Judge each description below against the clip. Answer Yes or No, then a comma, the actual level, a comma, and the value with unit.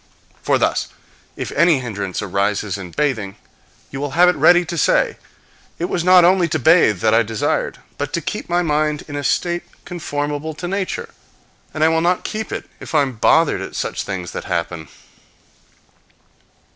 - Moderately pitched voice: Yes, medium, 150 Hz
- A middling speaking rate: Yes, average, 175 wpm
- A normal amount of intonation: No, wide, 7.9 semitones